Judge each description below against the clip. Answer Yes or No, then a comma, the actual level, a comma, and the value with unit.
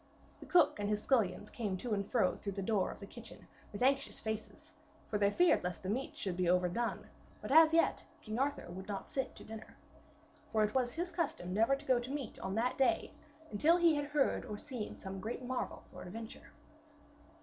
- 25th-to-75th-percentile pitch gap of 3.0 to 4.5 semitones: No, average, 5.3 semitones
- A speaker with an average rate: No, fast, 210 wpm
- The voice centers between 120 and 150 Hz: No, high, 225 Hz